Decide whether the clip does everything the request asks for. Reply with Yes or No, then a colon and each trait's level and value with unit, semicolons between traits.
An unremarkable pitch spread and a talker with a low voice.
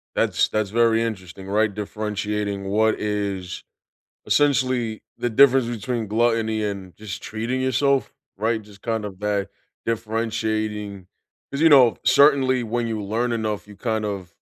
No: narrow, 2.3 semitones; low, 110 Hz